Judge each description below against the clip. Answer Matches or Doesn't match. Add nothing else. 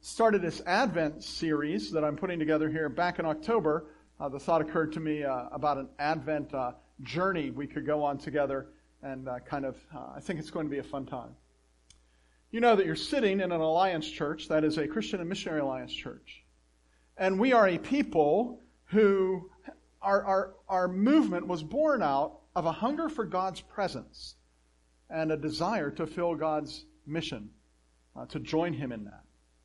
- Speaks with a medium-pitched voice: Matches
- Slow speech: Doesn't match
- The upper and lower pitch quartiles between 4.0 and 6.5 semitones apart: Matches